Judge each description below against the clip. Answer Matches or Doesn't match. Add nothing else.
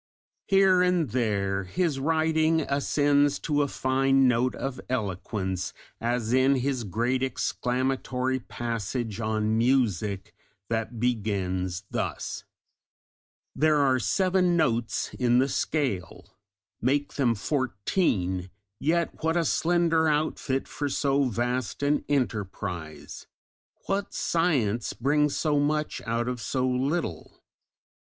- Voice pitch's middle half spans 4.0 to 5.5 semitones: Matches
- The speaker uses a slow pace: Matches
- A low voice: Matches